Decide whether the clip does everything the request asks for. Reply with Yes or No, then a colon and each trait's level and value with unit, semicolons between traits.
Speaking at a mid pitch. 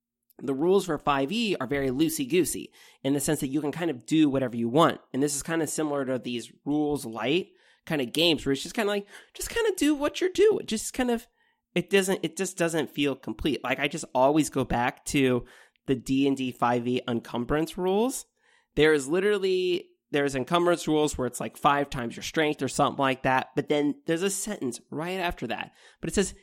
Yes: medium, 150 Hz